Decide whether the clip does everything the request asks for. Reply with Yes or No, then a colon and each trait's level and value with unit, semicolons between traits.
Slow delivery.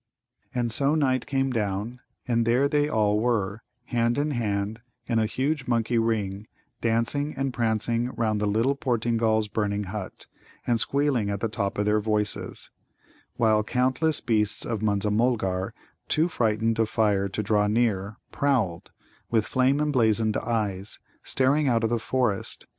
No: average, 155 wpm